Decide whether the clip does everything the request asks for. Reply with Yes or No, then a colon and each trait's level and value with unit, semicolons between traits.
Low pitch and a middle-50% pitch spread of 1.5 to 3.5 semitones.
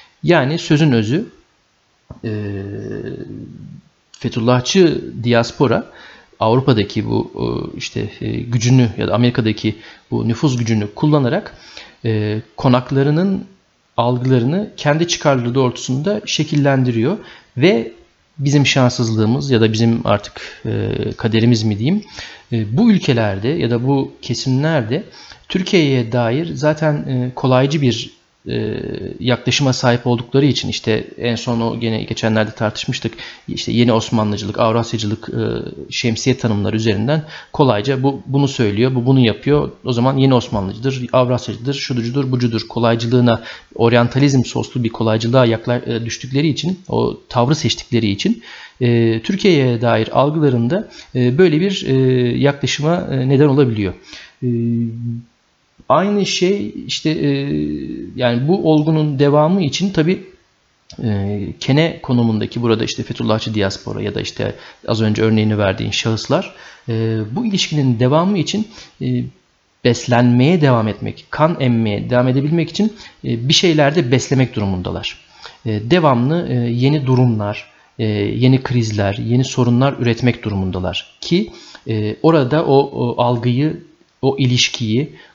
No: low, 125 Hz; average, 4.0 semitones